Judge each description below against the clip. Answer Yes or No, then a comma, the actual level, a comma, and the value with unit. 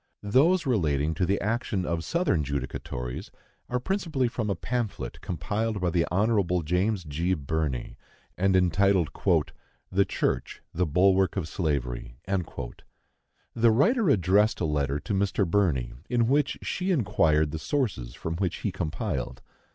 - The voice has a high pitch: No, very low, 95 Hz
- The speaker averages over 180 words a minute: No, average, 140 wpm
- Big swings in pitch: Yes, wide, 6.0 semitones